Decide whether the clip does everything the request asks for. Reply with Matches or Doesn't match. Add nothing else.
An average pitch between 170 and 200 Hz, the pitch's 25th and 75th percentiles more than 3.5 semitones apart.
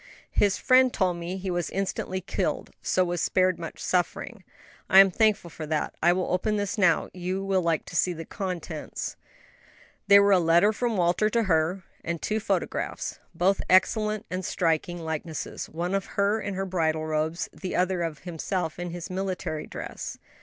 Doesn't match